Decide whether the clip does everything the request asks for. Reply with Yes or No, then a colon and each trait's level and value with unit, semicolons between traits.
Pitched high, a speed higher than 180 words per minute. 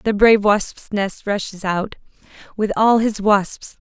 No: high, 205 Hz; average, 155 wpm